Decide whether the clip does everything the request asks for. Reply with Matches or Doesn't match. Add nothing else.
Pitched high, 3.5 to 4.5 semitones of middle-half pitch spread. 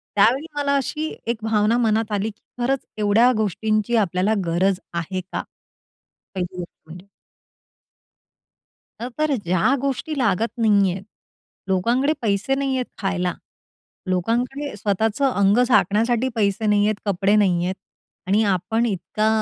Matches